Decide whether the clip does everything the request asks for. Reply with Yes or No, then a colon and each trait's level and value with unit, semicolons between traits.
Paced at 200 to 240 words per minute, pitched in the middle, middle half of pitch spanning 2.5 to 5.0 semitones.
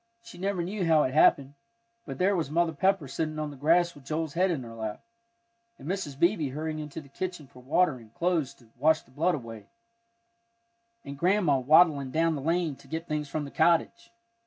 Yes: fast, 205 wpm; medium, 155 Hz; average, 3.8 semitones